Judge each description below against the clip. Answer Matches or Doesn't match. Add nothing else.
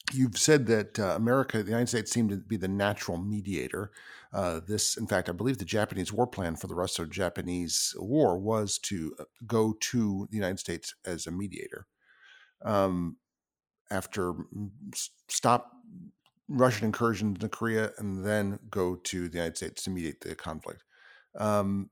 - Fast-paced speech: Doesn't match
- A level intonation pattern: Doesn't match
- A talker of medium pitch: Doesn't match